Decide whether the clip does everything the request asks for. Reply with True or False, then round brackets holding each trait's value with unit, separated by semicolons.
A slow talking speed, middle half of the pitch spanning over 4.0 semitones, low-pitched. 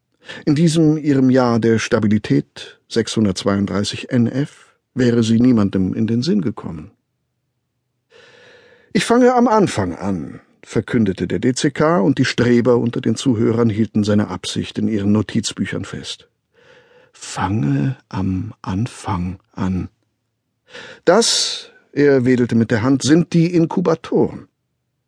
True (115 wpm; 5.0 semitones; 120 Hz)